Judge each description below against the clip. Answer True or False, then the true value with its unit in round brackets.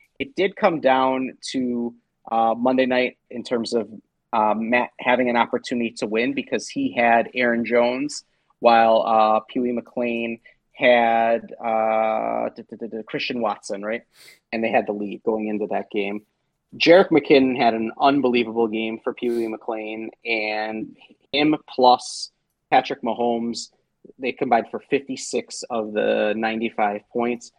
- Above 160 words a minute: False (140 wpm)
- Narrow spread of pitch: True (1.9 semitones)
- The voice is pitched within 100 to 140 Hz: True (115 Hz)